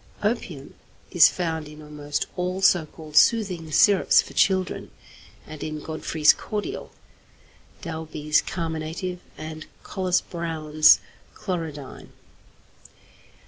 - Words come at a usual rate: No, slow, 100 wpm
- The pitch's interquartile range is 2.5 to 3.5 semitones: Yes, average, 2.9 semitones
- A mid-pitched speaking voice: Yes, medium, 160 Hz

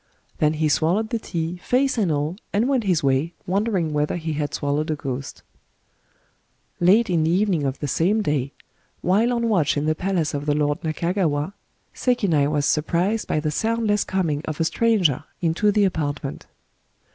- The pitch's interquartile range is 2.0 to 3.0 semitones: No, average, 5.3 semitones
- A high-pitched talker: No, medium, 165 Hz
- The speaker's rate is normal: Yes, average, 180 wpm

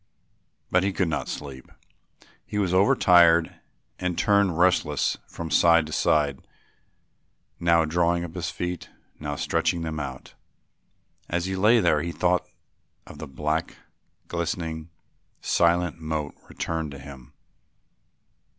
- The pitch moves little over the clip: Yes, narrow, 2.2 semitones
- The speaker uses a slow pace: Yes, slow, 125 wpm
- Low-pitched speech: Yes, very low, 85 Hz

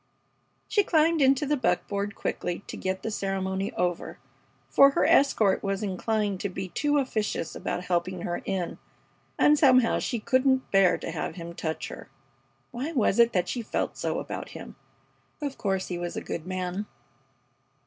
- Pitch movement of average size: No, wide, 6.1 semitones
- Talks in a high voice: Yes, high, 200 Hz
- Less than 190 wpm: Yes, average, 170 wpm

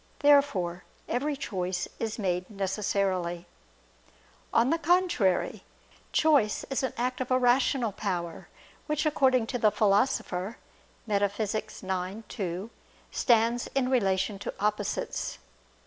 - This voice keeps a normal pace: No, slow, 115 wpm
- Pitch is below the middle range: No, high, 215 Hz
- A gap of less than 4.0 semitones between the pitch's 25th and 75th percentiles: No, average, 5.1 semitones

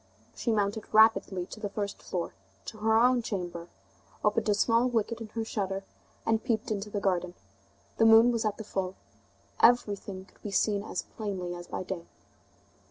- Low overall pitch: No, high, 210 Hz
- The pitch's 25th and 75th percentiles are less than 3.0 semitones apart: Yes, narrow, 2.6 semitones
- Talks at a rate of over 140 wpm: Yes, average, 175 wpm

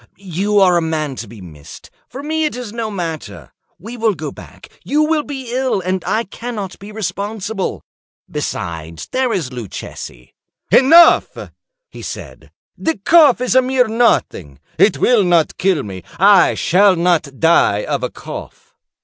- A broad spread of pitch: Yes, wide, 7.2 semitones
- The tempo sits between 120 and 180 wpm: Yes, average, 160 wpm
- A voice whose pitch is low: No, high, 200 Hz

